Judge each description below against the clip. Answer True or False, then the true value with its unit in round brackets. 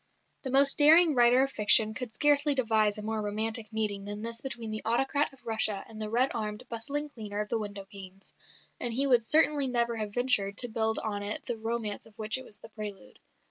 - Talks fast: True (220 wpm)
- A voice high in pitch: True (225 Hz)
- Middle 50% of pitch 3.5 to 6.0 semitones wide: False (3.1 semitones)